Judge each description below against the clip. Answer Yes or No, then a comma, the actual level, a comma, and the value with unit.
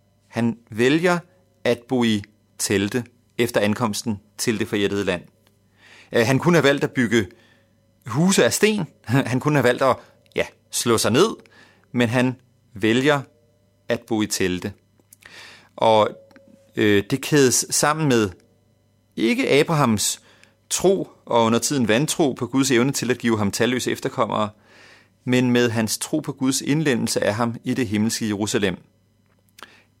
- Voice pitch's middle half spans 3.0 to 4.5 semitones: Yes, average, 3.4 semitones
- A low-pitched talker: Yes, low, 115 Hz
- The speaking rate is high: No, slow, 145 wpm